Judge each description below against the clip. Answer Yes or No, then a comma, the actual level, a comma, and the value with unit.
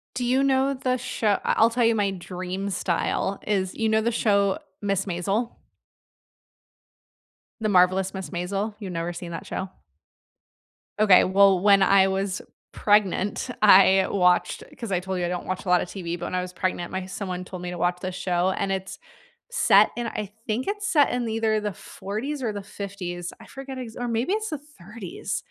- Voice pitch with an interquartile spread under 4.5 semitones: Yes, average, 3.5 semitones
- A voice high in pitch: Yes, high, 195 Hz